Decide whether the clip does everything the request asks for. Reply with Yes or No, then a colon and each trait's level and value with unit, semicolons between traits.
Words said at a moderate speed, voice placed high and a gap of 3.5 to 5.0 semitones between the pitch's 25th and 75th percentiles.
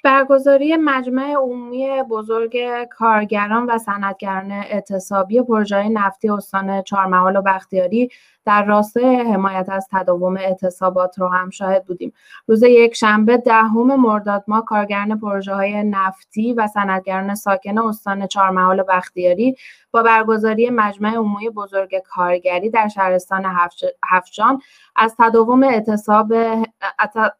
No: average, 115 wpm; high, 210 Hz; average, 3.1 semitones